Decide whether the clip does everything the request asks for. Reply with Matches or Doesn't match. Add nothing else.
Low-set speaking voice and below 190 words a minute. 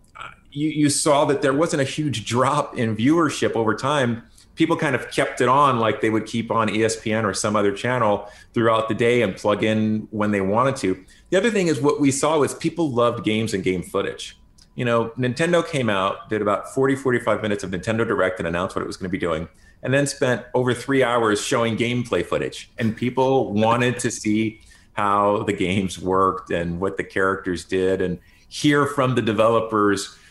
Doesn't match